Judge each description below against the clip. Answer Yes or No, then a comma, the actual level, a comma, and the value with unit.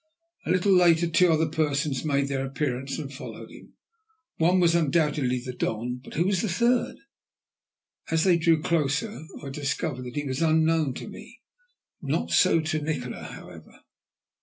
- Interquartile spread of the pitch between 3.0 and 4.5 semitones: Yes, average, 3.5 semitones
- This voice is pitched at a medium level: Yes, medium, 155 Hz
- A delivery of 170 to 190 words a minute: No, average, 160 wpm